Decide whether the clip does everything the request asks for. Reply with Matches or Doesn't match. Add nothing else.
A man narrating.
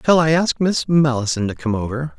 Matches